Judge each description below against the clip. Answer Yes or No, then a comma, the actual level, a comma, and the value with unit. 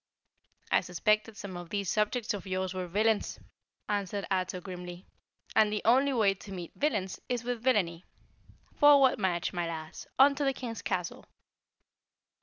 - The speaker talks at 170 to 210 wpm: No, average, 155 wpm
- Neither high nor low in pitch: No, high, 205 Hz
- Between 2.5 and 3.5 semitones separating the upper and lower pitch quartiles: No, average, 4.4 semitones